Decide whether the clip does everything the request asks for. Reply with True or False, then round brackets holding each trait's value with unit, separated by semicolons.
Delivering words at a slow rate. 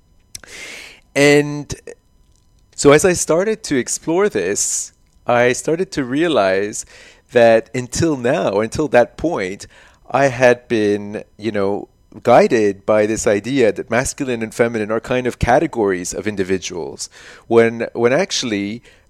True (125 wpm)